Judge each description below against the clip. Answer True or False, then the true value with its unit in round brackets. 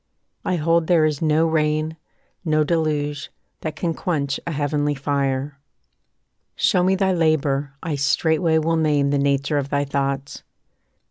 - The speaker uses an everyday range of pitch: False (2.3 semitones)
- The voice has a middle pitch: True (150 Hz)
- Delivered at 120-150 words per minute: True (145 wpm)